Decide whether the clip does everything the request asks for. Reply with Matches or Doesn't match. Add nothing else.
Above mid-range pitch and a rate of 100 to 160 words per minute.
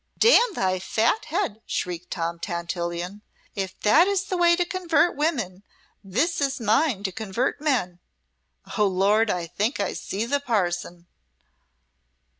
Matches